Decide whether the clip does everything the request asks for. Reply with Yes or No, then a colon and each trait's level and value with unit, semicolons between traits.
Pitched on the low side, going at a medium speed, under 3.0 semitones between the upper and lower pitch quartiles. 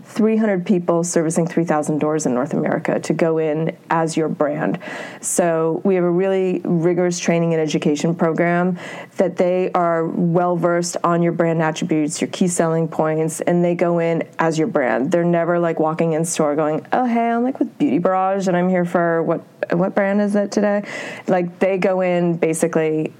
No: medium, 170 Hz; average, 190 wpm; narrow, 2.4 semitones